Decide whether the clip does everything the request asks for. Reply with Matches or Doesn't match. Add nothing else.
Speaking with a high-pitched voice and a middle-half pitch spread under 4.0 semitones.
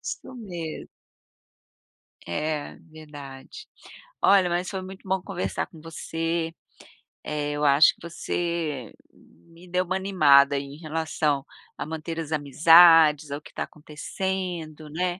Doesn't match